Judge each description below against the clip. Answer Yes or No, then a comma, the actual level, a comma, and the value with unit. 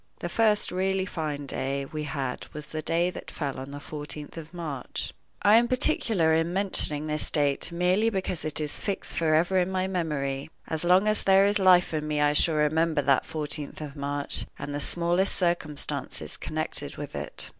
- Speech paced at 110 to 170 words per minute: No, average, 190 wpm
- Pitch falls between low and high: Yes, medium, 160 Hz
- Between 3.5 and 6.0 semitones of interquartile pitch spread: Yes, average, 4.0 semitones